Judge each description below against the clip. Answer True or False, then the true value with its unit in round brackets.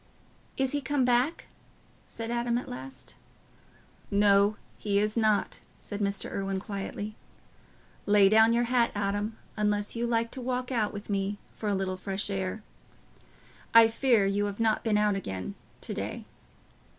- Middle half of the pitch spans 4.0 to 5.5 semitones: False (2.7 semitones)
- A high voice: True (210 Hz)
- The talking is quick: False (155 wpm)